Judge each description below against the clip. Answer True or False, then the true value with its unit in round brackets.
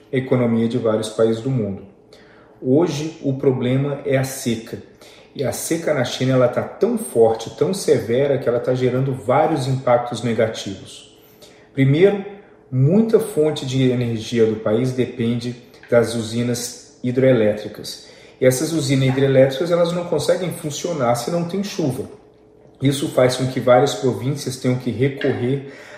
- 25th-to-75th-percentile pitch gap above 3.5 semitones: False (3.1 semitones)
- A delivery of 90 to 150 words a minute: True (145 wpm)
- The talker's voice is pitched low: True (130 Hz)